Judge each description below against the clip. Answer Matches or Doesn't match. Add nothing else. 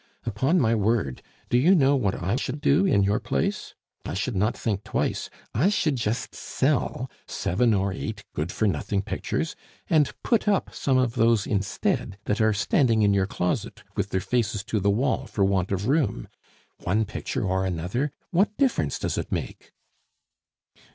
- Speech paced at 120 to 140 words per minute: Doesn't match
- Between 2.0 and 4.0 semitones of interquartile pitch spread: Doesn't match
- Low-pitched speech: Matches